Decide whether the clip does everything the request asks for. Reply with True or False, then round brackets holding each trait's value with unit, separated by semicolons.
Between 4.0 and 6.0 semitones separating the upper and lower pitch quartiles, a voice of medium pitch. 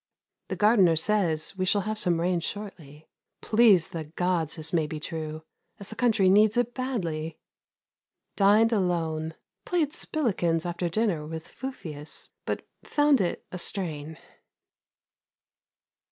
True (5.0 semitones; 180 Hz)